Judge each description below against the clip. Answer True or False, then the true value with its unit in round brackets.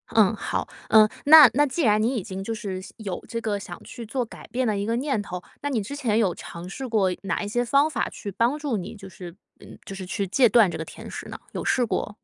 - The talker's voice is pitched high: True (220 Hz)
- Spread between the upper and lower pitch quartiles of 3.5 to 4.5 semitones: True (4.2 semitones)